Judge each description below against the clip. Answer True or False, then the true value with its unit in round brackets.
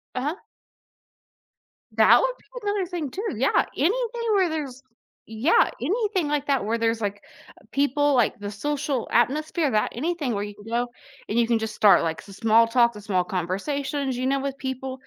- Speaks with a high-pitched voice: True (260 Hz)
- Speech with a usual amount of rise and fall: True (5.0 semitones)